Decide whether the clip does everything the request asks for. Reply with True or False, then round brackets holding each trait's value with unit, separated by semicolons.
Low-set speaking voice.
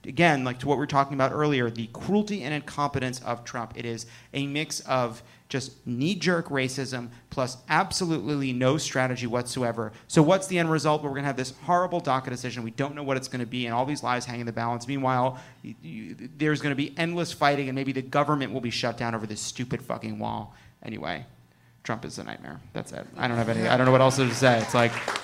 True (130 Hz)